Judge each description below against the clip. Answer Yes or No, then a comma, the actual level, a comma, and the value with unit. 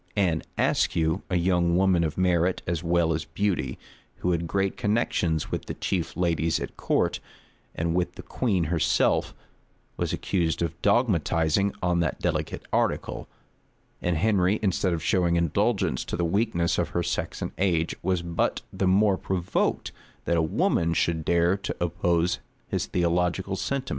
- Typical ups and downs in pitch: No, narrow, 2.2 semitones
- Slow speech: No, average, 160 wpm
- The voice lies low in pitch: Yes, very low, 85 Hz